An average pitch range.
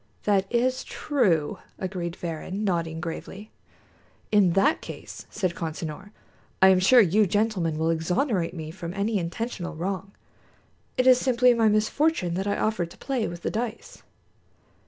Yes: average, 4.5 semitones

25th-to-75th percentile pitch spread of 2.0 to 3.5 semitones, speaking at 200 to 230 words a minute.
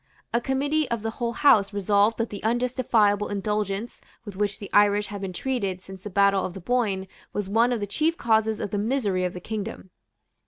Yes: average, 2.9 semitones; fast, 205 wpm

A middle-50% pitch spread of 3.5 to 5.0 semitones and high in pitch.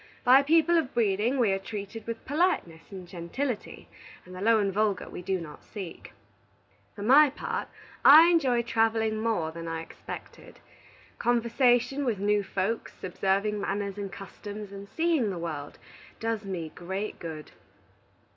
Yes: average, 4.1 semitones; high, 210 Hz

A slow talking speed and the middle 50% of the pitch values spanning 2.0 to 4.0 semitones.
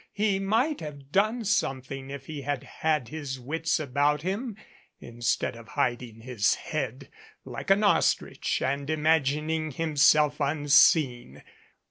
Yes: slow, 130 wpm; average, 3.4 semitones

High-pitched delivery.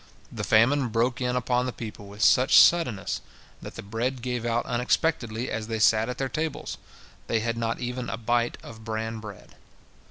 No: low, 120 Hz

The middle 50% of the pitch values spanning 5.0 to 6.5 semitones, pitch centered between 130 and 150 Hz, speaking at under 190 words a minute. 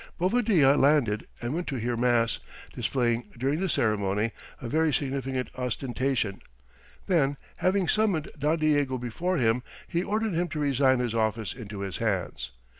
Yes: wide, 5.4 semitones; low, 135 Hz; average, 150 wpm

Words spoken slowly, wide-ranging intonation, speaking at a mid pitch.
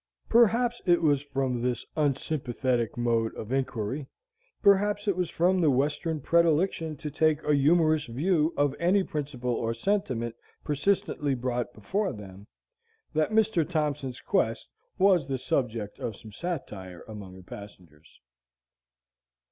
Yes: slow, 130 wpm; wide, 6.1 semitones; medium, 145 Hz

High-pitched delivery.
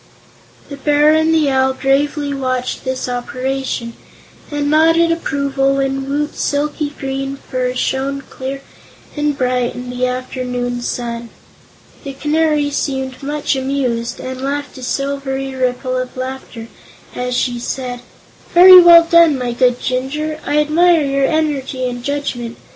Yes: very high, 270 Hz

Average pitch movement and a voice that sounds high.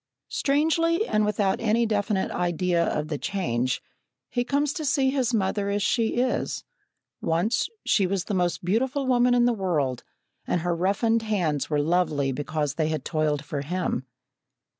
No: wide, 7.2 semitones; high, 195 Hz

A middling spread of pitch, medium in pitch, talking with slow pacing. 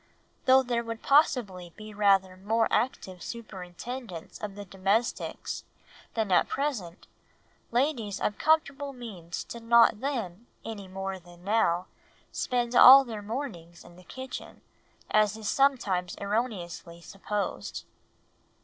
No: average, 4.6 semitones; high, 215 Hz; slow, 120 wpm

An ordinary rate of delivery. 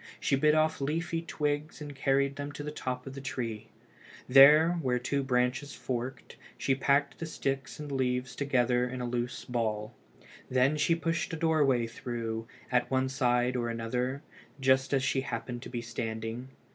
Yes: average, 170 wpm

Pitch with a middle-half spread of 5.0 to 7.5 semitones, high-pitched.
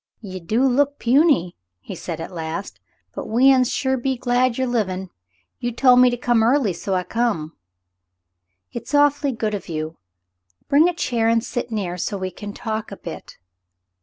Yes: wide, 5.4 semitones; high, 230 Hz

